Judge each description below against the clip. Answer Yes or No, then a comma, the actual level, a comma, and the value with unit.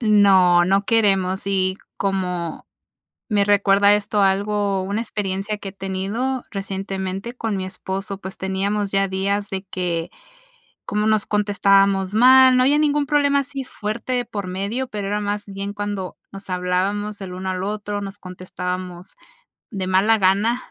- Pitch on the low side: No, high, 200 Hz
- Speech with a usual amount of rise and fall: No, narrow, 1.8 semitones